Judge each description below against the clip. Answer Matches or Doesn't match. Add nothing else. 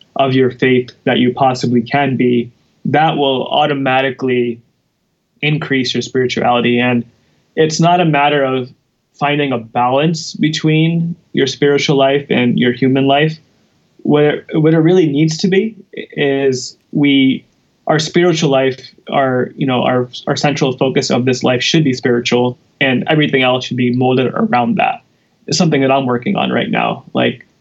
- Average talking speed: Matches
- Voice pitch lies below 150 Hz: Matches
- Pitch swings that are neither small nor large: Matches